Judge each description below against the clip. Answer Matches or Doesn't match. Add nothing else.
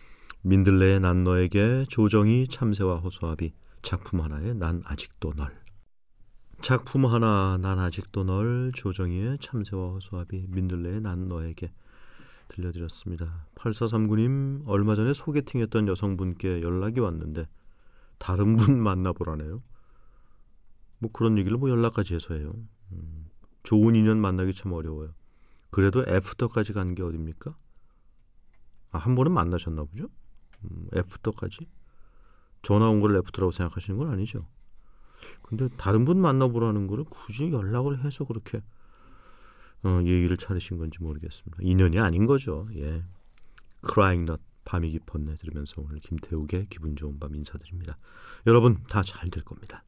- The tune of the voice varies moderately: Matches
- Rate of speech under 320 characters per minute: Matches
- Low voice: Matches